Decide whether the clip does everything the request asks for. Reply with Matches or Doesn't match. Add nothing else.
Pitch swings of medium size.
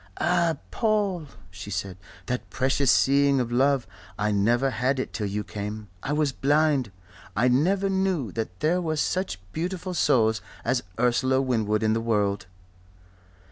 Doesn't match